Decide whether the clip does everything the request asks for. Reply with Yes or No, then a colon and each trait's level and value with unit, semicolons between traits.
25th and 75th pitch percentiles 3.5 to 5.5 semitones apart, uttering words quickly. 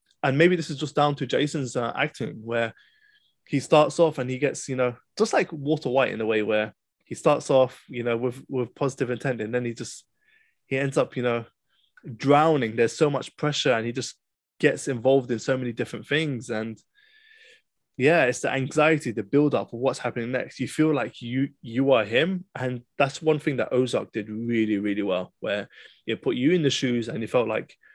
Yes: average, 4.0 semitones; fast, 215 wpm